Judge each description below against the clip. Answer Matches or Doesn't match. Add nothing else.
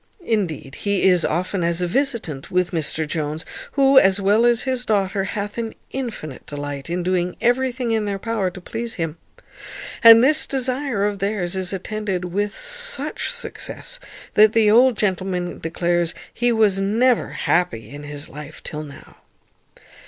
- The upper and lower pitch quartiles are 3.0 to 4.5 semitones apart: Doesn't match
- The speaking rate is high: Doesn't match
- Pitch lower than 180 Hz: Doesn't match